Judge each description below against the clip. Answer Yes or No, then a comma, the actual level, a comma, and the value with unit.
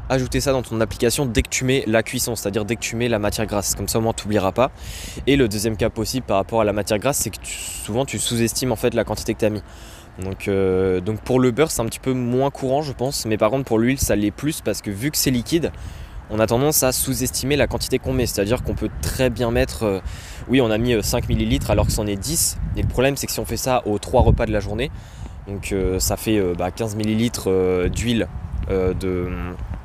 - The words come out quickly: Yes, fast, 265 wpm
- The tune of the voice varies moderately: Yes, average, 3.9 semitones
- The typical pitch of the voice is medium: No, low, 110 Hz